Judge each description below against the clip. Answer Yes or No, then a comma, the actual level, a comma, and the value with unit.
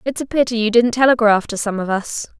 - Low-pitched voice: No, high, 230 Hz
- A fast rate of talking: Yes, fast, 250 wpm